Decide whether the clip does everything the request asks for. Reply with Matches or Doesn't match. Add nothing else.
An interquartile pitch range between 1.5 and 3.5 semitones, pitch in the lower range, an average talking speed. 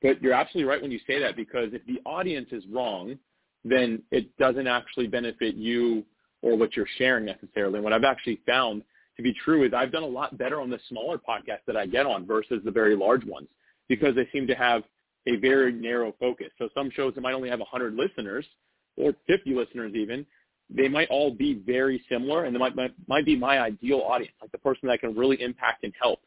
Doesn't match